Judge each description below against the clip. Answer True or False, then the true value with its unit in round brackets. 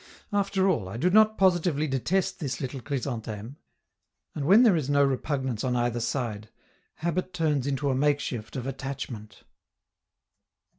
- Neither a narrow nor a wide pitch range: False (5.7 semitones)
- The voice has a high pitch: False (140 Hz)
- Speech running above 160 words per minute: False (145 wpm)